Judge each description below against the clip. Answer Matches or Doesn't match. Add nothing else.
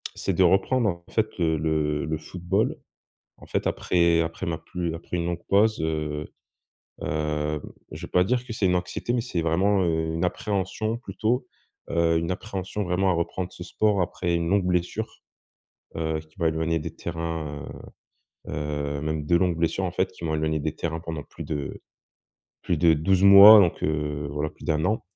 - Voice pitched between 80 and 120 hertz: Matches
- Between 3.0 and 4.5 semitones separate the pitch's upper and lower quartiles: Matches